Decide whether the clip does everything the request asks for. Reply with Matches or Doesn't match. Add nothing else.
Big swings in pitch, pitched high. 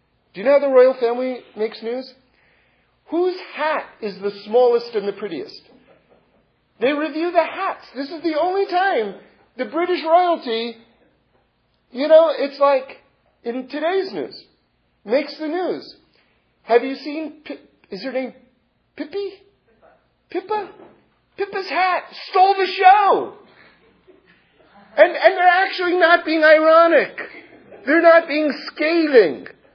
Matches